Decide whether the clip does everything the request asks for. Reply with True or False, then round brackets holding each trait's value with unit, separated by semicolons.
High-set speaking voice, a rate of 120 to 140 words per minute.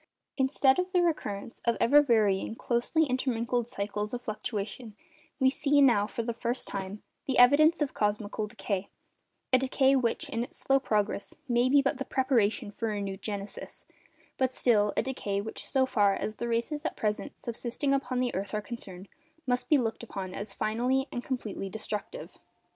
False (235 Hz; 170 wpm)